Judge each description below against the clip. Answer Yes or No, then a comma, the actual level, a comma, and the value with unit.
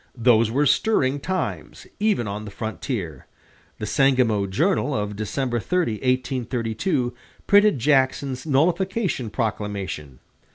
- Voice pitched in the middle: No, low, 125 Hz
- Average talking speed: No, slow, 110 wpm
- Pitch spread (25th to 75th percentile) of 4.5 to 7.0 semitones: Yes, average, 5.2 semitones